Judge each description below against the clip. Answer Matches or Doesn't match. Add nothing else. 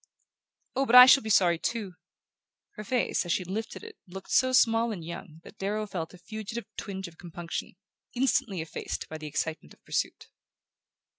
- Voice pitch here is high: Matches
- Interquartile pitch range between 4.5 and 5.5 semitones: Matches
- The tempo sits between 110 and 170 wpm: Doesn't match